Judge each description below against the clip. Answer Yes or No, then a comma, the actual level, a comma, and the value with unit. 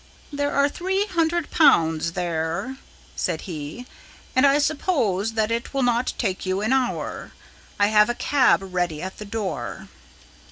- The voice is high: Yes, high, 230 Hz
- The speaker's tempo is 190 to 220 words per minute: No, average, 160 wpm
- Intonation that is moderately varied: No, wide, 7.2 semitones